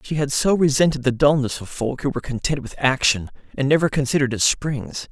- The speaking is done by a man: Yes, male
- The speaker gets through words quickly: Yes, fast, 210 wpm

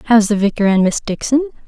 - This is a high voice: Yes, high, 220 Hz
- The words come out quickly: Yes, fast, 215 wpm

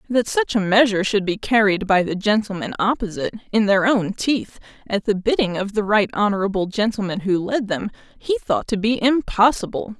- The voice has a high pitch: Yes, high, 210 Hz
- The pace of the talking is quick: No, average, 185 wpm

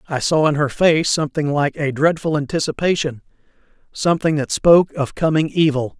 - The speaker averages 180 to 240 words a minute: No, average, 150 wpm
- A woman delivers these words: No, male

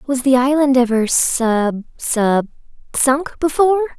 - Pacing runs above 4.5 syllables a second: No, 4.0 syllables/s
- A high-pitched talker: Yes, very high, 260 Hz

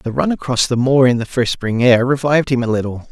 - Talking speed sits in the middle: No, fast, 270 wpm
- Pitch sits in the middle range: No, low, 125 Hz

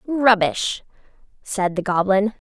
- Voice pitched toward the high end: Yes, high, 205 Hz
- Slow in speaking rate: Yes, slow, 95 wpm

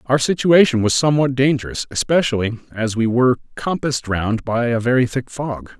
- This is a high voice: No, low, 125 Hz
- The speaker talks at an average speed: Yes, average, 165 wpm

